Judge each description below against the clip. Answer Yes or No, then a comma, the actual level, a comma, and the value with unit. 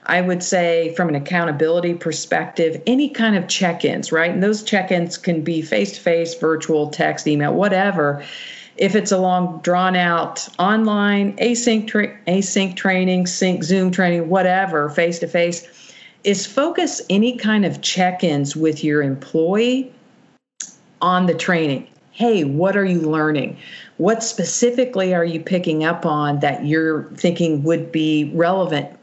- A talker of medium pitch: Yes, medium, 180 Hz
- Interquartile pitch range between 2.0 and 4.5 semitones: Yes, average, 3.6 semitones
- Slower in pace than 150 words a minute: Yes, average, 140 wpm